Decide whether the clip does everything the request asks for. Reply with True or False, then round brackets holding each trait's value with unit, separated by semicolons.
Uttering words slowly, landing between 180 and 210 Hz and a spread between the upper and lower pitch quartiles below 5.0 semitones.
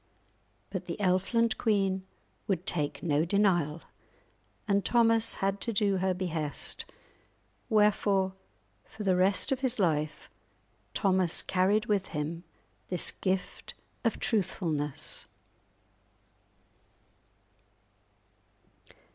True (95 wpm; 190 Hz; 3.2 semitones)